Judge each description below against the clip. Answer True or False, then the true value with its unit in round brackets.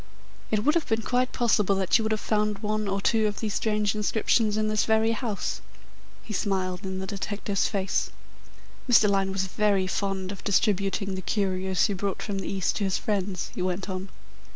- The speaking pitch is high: True (200 Hz)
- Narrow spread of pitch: True (2.0 semitones)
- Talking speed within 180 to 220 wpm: True (200 wpm)